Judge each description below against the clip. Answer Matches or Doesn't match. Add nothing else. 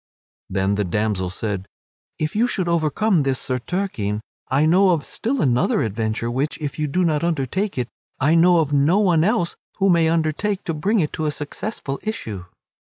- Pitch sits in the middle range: Matches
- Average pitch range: Doesn't match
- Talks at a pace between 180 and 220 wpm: Matches